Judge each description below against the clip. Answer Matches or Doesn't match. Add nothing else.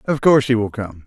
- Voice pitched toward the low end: Matches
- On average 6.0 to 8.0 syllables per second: Matches